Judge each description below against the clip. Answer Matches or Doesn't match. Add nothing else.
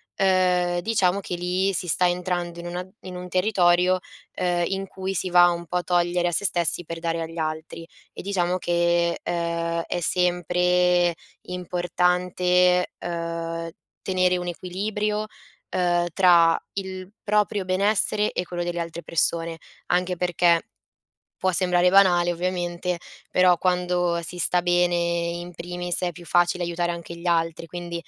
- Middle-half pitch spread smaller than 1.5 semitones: Matches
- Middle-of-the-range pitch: Matches